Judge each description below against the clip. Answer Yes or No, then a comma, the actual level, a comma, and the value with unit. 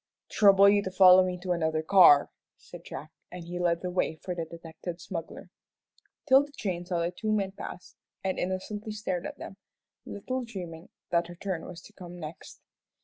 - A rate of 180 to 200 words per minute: Yes, average, 185 wpm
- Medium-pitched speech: Yes, medium, 180 Hz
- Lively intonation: No, narrow, 2.6 semitones